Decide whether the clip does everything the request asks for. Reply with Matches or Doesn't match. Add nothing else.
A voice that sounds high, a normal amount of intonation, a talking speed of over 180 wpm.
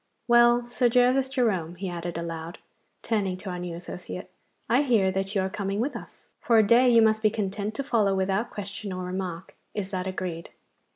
Matches